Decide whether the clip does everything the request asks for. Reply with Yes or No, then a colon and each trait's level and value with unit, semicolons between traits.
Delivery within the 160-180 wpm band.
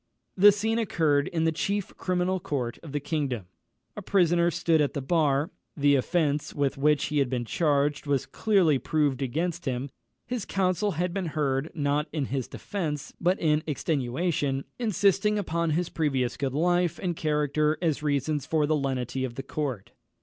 Yes: average, 170 wpm